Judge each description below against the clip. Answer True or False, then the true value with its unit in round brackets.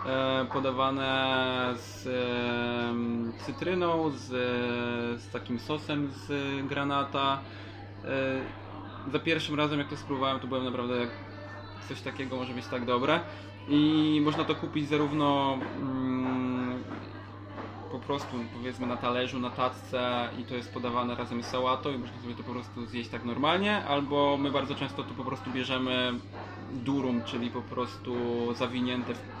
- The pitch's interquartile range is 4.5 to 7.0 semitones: False (2.4 semitones)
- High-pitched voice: False (125 Hz)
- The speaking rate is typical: True (135 wpm)